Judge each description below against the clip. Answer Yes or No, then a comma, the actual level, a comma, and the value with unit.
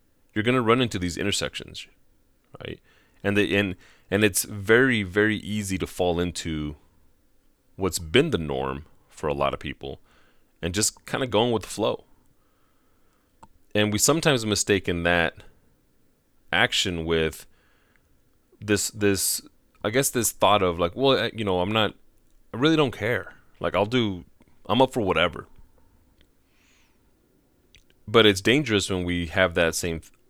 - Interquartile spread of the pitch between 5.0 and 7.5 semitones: No, average, 4.0 semitones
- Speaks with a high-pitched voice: No, very low, 95 Hz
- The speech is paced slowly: No, average, 150 wpm